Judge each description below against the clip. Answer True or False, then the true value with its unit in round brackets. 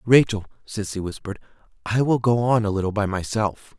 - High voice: False (110 Hz)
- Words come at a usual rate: True (175 wpm)